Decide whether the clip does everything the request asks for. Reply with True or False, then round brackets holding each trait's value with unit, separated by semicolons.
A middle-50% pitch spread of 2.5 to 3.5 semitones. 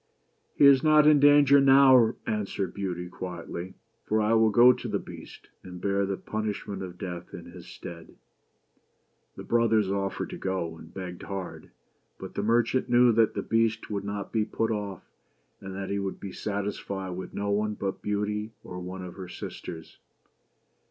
True (3.2 semitones)